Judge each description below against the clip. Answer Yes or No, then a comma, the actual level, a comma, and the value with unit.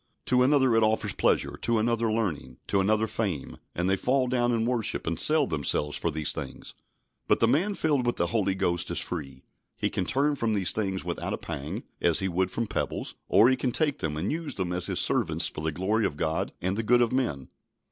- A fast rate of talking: Yes, fast, 230 wpm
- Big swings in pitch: Yes, wide, 5.9 semitones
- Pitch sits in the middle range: No, low, 110 Hz